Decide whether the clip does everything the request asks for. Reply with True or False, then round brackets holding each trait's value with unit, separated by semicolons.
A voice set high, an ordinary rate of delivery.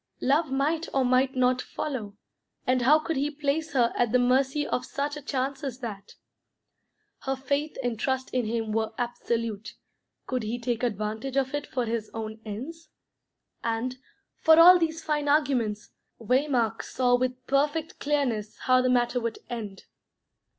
True (255 Hz; 160 wpm)